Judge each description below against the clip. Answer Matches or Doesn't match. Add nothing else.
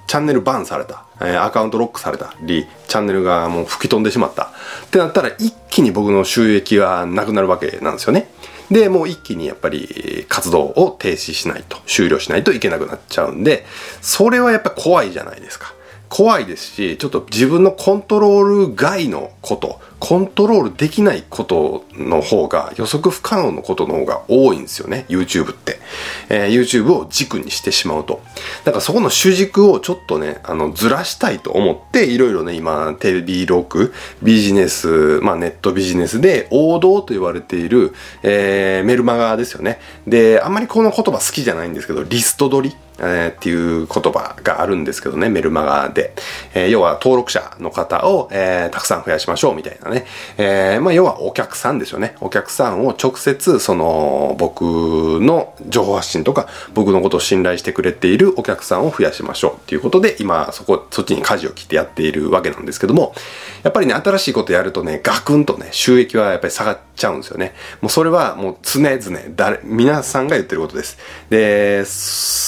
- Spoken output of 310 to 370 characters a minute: Doesn't match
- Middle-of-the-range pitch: Doesn't match